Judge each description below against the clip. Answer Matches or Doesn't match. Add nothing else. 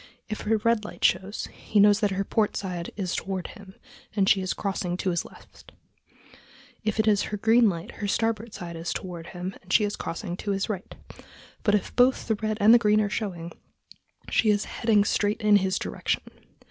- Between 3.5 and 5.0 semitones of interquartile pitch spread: Doesn't match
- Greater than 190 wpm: Matches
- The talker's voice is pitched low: Doesn't match